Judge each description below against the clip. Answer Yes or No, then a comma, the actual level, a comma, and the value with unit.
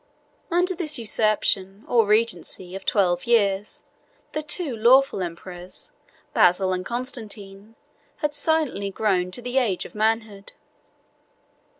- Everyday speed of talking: No, slow, 120 wpm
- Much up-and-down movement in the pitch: No, average, 4.3 semitones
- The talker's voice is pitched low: No, high, 215 Hz